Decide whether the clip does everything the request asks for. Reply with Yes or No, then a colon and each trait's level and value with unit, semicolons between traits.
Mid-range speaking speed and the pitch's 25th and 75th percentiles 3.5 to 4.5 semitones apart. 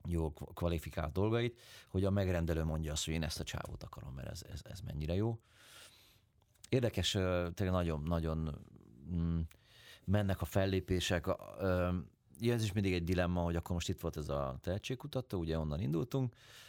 No: fast, 160 wpm; average, 4.0 semitones